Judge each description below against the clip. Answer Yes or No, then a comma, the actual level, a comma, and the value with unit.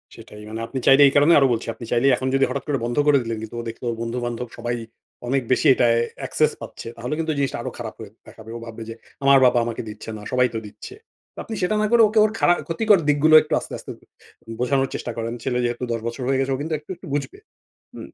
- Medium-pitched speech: No, low, 125 Hz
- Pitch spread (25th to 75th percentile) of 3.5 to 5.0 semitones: Yes, average, 3.9 semitones